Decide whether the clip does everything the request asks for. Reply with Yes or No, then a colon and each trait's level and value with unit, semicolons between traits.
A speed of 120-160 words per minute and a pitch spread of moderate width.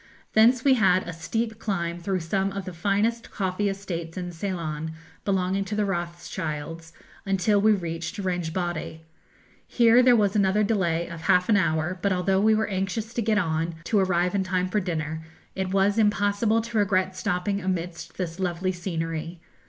No: average, 170 wpm; average, 3.1 semitones